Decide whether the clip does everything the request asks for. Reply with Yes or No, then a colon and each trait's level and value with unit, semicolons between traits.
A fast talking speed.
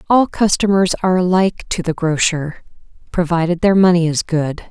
No: average, 155 wpm